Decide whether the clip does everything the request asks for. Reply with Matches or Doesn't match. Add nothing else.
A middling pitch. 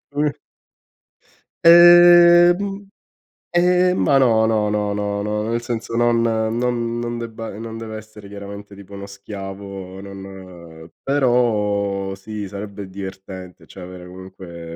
Doesn't match